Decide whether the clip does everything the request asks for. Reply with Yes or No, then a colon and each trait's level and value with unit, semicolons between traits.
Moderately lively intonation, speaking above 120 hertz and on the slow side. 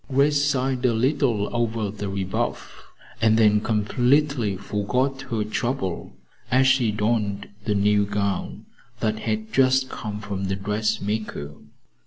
No: average, 3.8 semitones; low, 110 Hz; slow, 130 wpm